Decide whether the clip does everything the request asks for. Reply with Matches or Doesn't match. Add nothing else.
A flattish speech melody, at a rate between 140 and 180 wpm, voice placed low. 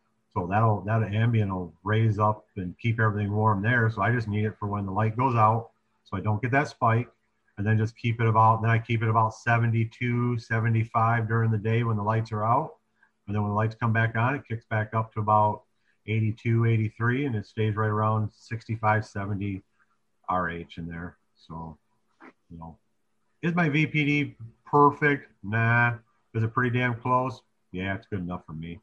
Doesn't match